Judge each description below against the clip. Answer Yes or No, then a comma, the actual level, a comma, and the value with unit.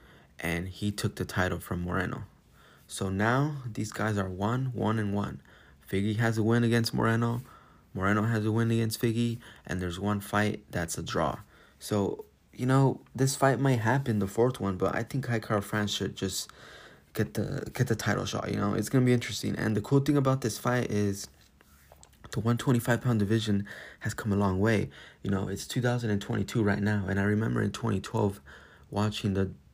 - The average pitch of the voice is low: Yes, low, 105 Hz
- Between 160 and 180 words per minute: No, fast, 205 wpm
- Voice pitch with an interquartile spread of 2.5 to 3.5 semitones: Yes, average, 3.1 semitones